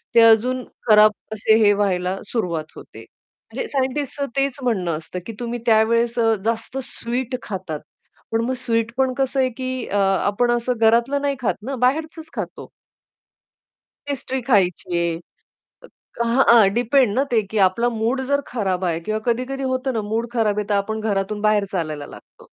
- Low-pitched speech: No, high, 230 Hz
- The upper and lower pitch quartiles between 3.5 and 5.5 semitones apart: Yes, average, 3.8 semitones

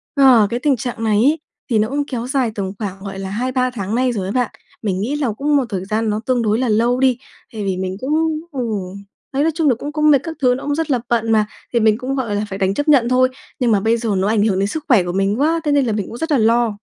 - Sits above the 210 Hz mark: Yes, high, 235 Hz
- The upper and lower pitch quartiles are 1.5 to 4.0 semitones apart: No, average, 4.4 semitones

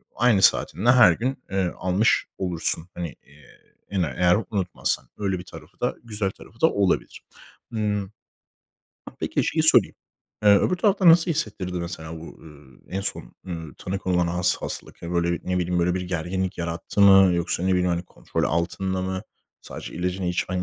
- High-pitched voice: No, very low, 90 Hz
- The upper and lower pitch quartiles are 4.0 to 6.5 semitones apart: No, narrow, 2.6 semitones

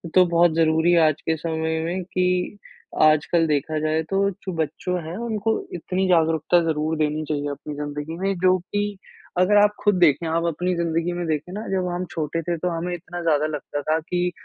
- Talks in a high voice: No, medium, 165 Hz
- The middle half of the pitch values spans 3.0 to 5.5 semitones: No, narrow, 2.5 semitones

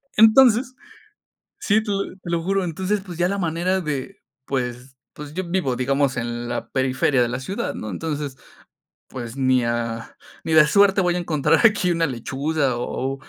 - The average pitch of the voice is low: No, medium, 150 Hz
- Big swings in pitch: Yes, wide, 6.4 semitones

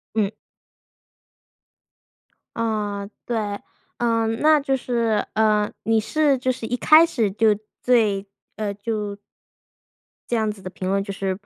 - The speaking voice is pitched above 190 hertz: Yes, high, 220 Hz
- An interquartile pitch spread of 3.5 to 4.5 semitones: No, average, 2.9 semitones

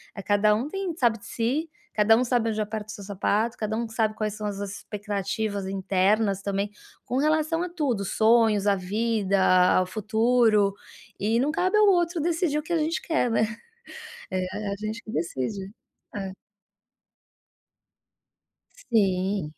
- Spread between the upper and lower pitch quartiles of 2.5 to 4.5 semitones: Yes, average, 3.7 semitones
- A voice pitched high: Yes, high, 215 Hz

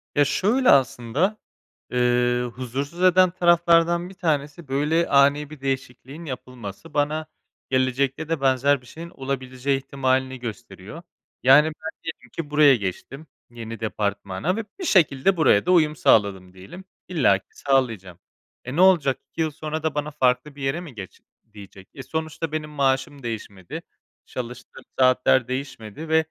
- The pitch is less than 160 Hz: Yes, medium, 140 Hz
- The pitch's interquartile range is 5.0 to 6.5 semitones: No, average, 4.2 semitones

